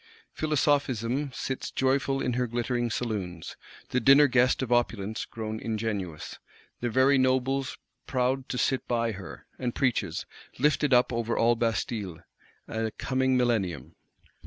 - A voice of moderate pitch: No, low, 120 Hz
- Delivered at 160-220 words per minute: No, slow, 135 wpm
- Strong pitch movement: No, average, 2.8 semitones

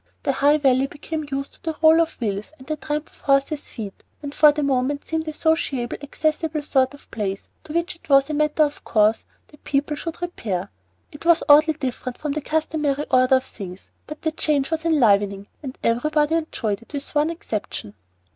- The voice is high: Yes, very high, 290 Hz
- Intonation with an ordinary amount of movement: Yes, average, 3.3 semitones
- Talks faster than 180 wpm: Yes, average, 200 wpm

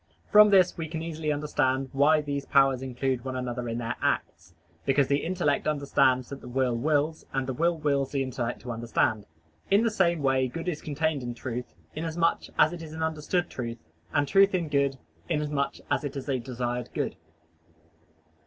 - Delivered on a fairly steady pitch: No, average, 3.7 semitones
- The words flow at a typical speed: Yes, average, 190 wpm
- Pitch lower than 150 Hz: Yes, medium, 140 Hz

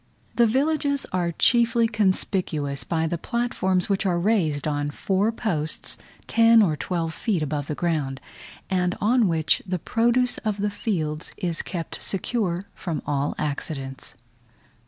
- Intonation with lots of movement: Yes, wide, 6.1 semitones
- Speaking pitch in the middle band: Yes, medium, 180 Hz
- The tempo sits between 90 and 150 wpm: Yes, average, 140 wpm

